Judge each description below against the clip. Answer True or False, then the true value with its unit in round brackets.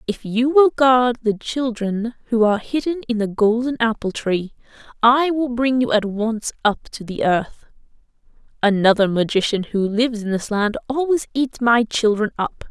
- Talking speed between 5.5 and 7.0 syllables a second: False (4.6 syllables/s)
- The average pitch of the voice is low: False (230 Hz)